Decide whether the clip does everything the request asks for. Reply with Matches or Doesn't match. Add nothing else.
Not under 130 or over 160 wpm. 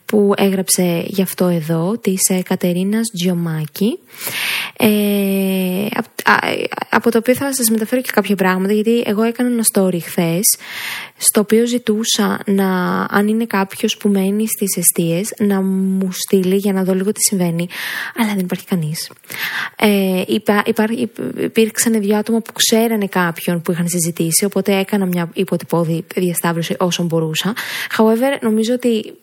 Matches